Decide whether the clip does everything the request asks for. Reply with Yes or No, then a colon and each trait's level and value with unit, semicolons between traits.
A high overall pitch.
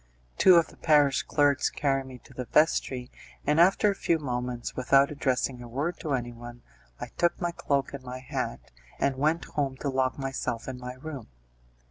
No: low, 135 Hz